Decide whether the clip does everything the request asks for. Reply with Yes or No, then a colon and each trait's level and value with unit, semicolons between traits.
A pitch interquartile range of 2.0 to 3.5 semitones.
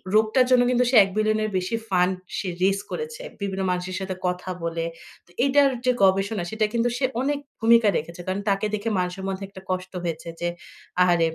No: average, 4.0 semitones